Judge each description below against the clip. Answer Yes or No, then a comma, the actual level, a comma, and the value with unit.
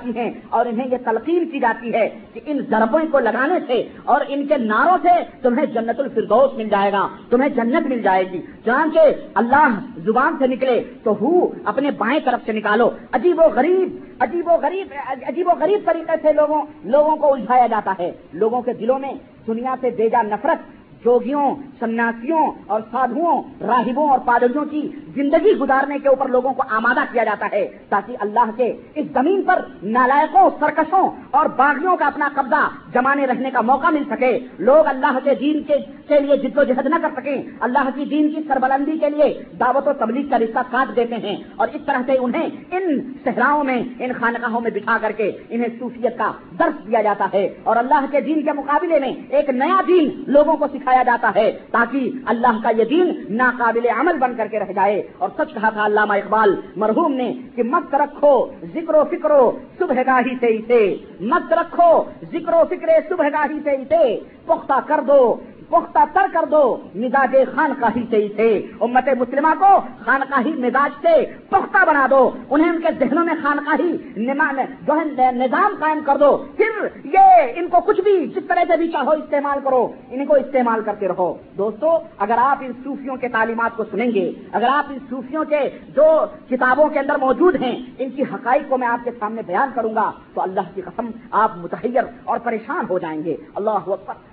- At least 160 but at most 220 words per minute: Yes, fast, 190 wpm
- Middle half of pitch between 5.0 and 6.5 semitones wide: No, average, 4.4 semitones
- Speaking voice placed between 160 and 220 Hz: No, very high, 270 Hz